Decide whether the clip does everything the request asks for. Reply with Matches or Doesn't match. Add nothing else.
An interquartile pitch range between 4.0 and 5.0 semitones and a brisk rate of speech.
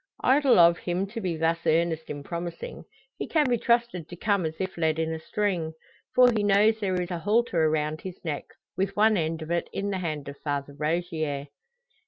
Matches